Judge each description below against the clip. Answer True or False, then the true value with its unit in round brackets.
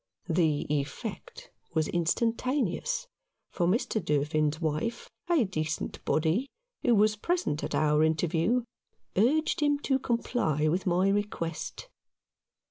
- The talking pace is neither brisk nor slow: False (115 wpm)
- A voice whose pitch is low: False (180 Hz)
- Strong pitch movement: True (7.3 semitones)